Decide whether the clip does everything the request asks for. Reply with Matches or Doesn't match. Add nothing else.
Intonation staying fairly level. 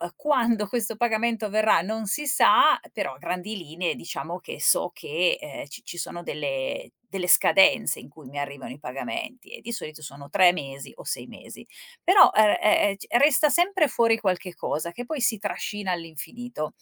Doesn't match